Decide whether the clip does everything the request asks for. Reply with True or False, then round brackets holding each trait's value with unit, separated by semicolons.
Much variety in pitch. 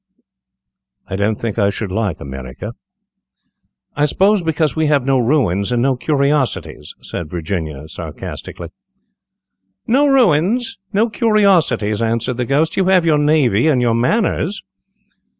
True (7.7 semitones)